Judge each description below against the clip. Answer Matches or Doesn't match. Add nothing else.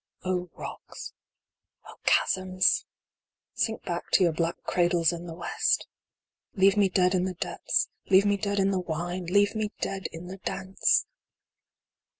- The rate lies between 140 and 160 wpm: Matches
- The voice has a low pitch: Doesn't match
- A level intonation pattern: Matches